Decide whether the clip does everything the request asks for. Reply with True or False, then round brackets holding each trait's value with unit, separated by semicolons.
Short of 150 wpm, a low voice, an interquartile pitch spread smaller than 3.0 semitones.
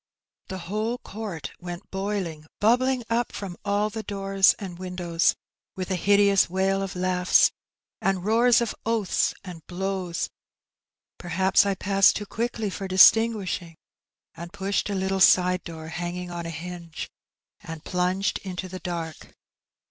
False (140 wpm; 190 Hz; 2.4 semitones)